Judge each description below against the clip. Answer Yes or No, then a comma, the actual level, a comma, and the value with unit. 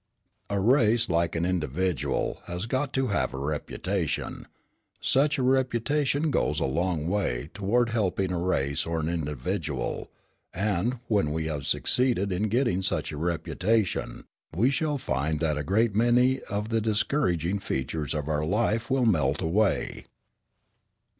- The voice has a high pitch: No, very low, 95 Hz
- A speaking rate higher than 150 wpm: No, average, 145 wpm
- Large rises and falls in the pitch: Yes, wide, 6.6 semitones